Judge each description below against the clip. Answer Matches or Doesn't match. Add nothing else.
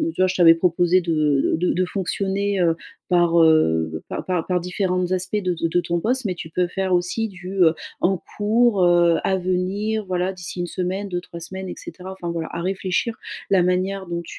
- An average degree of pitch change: Doesn't match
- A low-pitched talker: Doesn't match